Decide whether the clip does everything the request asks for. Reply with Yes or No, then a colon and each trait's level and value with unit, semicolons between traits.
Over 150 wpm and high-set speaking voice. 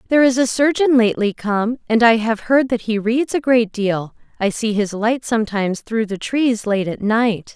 Yes: fast, 205 wpm; high, 225 Hz